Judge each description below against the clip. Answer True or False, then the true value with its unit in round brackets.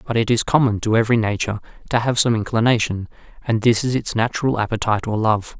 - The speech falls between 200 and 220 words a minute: True (205 wpm)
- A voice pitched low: True (115 Hz)